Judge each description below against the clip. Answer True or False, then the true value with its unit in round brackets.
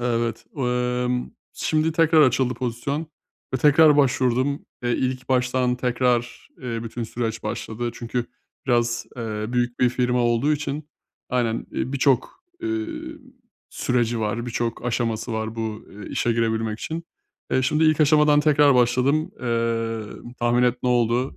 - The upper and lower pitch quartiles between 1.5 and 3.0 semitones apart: True (2.7 semitones)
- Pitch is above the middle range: False (125 Hz)